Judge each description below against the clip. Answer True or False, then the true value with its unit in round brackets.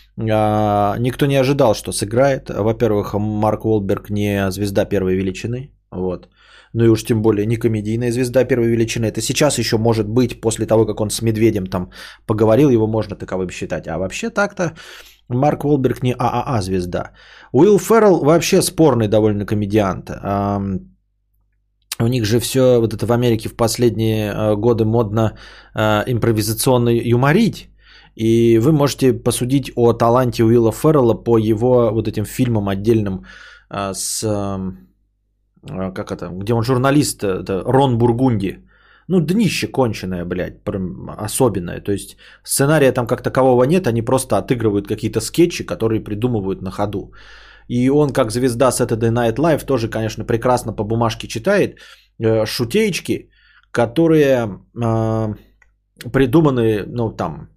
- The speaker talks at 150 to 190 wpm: False (140 wpm)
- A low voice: True (115 Hz)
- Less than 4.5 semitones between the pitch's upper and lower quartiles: True (3.3 semitones)